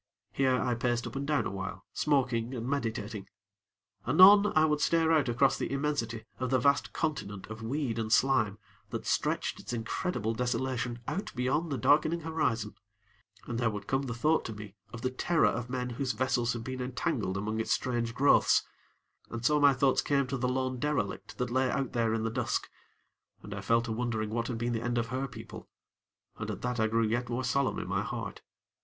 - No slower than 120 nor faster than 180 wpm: No, fast, 205 wpm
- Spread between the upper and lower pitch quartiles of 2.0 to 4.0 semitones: Yes, average, 3.2 semitones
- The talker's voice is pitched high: No, low, 125 Hz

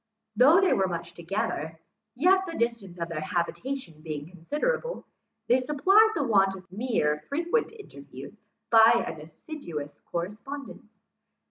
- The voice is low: No, high, 220 Hz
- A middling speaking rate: No, slow, 130 wpm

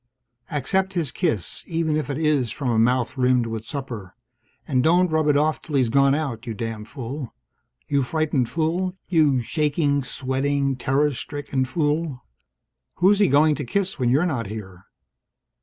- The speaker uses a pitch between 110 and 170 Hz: Yes, medium, 140 Hz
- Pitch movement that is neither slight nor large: Yes, average, 3.9 semitones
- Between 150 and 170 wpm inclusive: Yes, average, 165 wpm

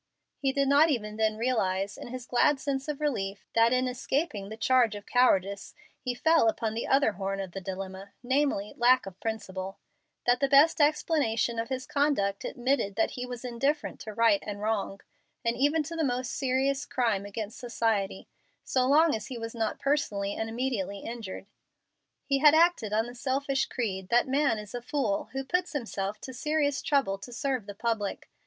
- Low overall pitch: No, high, 240 Hz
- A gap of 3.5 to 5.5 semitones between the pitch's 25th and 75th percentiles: Yes, average, 4.9 semitones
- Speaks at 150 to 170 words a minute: No, average, 190 wpm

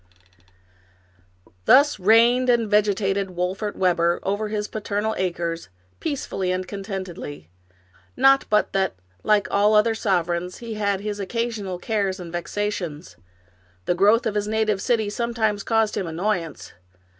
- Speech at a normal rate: No, slow, 130 wpm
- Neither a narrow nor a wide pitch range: Yes, average, 3.0 semitones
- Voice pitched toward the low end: No, high, 205 Hz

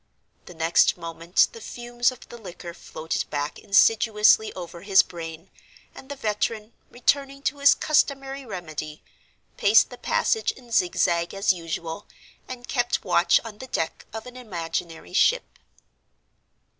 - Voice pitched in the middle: No, high, 205 Hz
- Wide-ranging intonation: Yes, wide, 6.2 semitones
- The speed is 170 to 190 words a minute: No, average, 140 wpm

